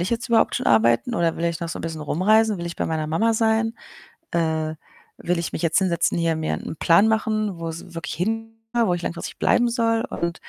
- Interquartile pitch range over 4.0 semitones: Yes, average, 5.1 semitones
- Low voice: No, medium, 170 Hz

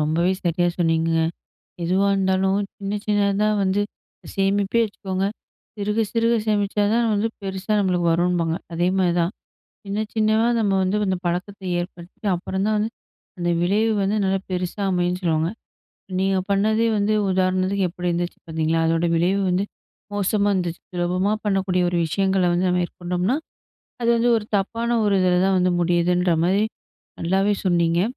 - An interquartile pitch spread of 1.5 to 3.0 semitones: Yes, narrow, 2.5 semitones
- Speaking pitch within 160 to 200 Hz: Yes, high, 190 Hz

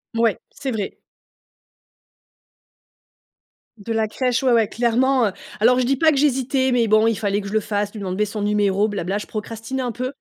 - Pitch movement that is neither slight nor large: Yes, average, 3.4 semitones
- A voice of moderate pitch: No, high, 225 Hz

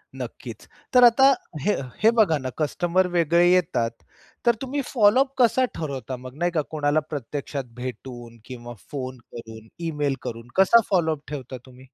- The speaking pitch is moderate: Yes, medium, 150 Hz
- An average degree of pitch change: No, wide, 6.7 semitones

